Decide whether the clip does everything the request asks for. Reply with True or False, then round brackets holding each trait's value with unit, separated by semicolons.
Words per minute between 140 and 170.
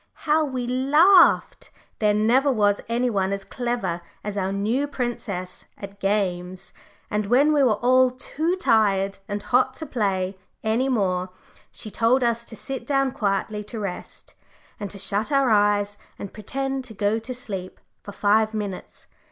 True (160 wpm)